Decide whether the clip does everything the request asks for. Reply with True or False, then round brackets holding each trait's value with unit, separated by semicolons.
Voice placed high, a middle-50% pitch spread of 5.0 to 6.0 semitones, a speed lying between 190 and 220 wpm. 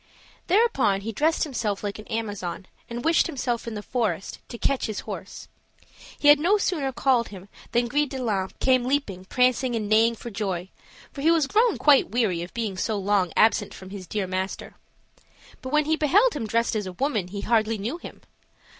True (230 Hz; 5.5 semitones; 200 wpm)